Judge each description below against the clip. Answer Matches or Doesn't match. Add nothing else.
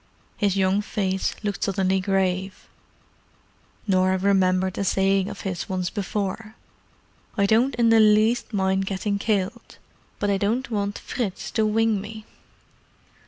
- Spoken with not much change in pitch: Matches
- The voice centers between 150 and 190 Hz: Doesn't match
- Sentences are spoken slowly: Matches